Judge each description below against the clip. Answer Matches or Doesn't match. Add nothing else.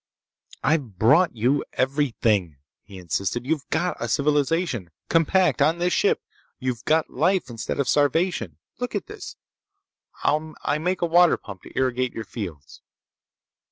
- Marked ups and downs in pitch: Matches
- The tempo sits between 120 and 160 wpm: Matches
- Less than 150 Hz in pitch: Matches